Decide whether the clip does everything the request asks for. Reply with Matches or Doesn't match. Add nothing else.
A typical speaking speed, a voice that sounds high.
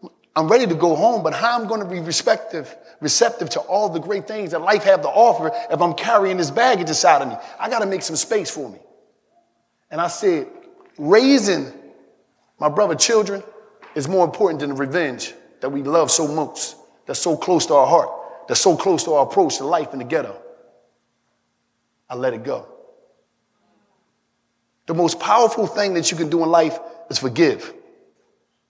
Matches